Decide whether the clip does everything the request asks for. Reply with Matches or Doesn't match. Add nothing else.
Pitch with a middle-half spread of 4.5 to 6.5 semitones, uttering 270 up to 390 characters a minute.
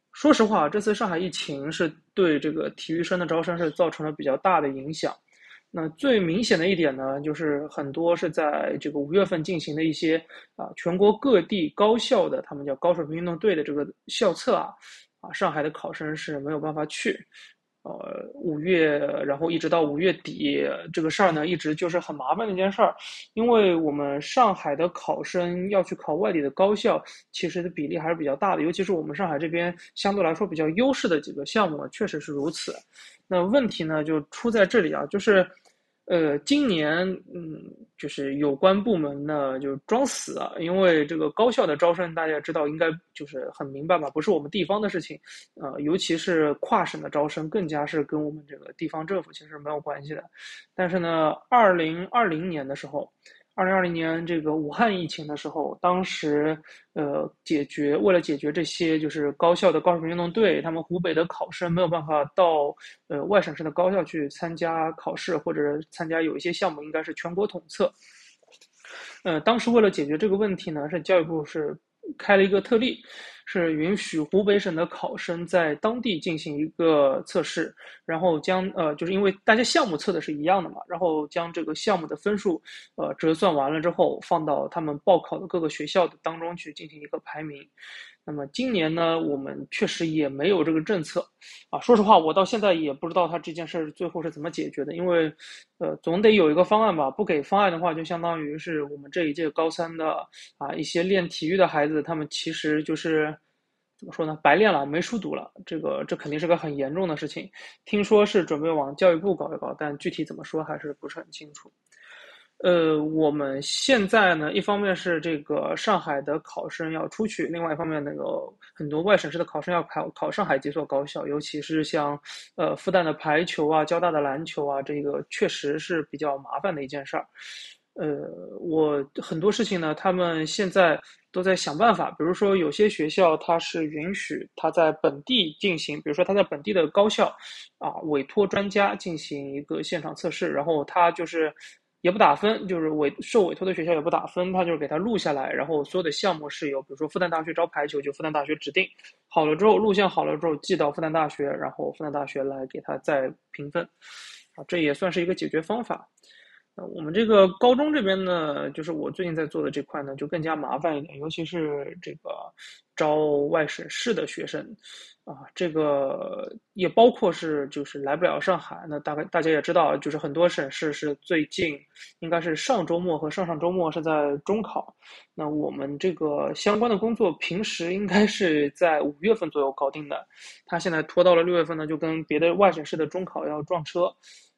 Doesn't match